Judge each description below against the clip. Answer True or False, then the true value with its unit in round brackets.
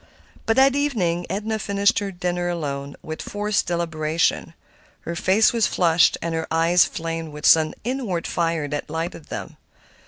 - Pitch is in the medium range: True (170 Hz)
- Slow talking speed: False (155 wpm)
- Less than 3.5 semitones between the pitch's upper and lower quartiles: False (3.8 semitones)